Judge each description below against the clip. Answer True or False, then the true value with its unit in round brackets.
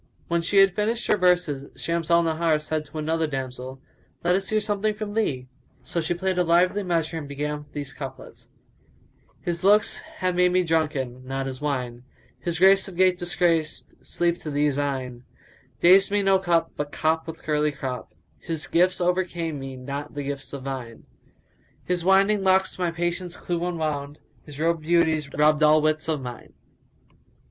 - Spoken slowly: False (180 wpm)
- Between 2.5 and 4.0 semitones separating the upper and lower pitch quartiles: True (3.7 semitones)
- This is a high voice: False (165 Hz)